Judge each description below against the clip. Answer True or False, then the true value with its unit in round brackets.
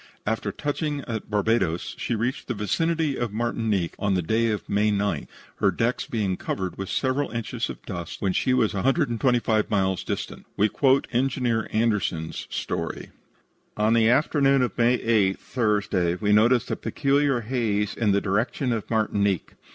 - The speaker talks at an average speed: True (165 wpm)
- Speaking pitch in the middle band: False (110 Hz)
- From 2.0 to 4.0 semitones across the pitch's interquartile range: True (3.6 semitones)